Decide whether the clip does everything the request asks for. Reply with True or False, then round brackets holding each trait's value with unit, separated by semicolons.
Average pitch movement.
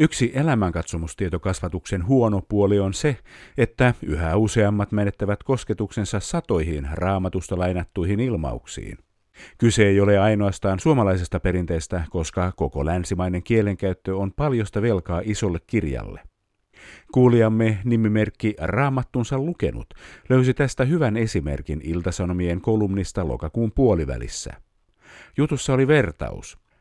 True (4.6 semitones)